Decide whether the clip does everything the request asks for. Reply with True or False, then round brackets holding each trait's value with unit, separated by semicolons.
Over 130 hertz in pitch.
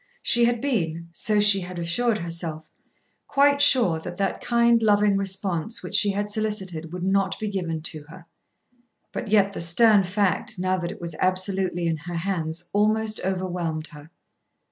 True (190 Hz)